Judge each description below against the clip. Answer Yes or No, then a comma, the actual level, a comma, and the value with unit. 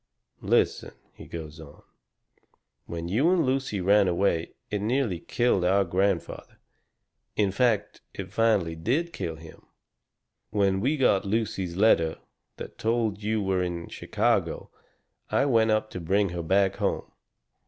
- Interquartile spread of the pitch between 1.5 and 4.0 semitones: No, average, 4.4 semitones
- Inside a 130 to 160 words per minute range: Yes, average, 140 wpm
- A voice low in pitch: Yes, low, 100 Hz